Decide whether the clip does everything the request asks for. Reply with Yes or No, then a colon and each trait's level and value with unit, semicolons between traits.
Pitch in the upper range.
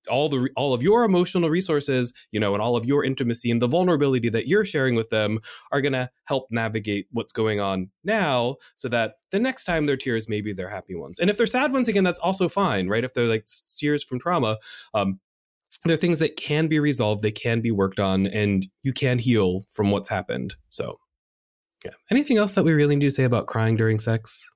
No: low, 125 Hz